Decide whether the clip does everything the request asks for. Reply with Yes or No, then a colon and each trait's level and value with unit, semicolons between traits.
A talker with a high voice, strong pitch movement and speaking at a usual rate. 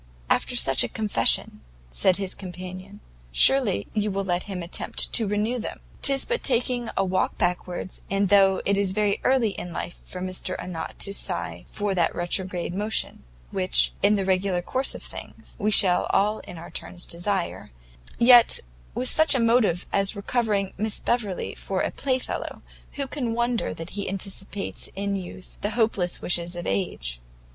No: high, 195 Hz; average, 3.4 semitones; average, 170 wpm